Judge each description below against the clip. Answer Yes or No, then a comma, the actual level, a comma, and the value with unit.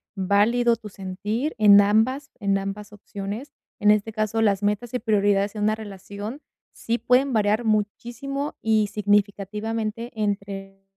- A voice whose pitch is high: Yes, high, 210 Hz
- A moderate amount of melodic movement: No, narrow, 2.1 semitones